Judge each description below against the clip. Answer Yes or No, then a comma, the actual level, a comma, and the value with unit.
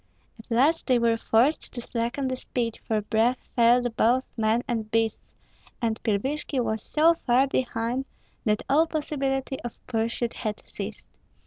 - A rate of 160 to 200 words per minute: No, average, 150 wpm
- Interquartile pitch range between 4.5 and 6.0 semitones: No, average, 2.9 semitones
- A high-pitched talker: Yes, high, 240 Hz